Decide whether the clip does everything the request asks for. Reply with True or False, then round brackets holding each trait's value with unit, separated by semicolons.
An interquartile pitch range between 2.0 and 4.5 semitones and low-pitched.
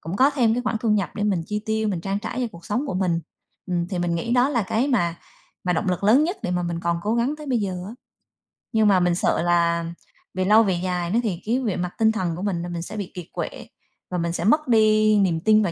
False (4.2 semitones; 200 Hz)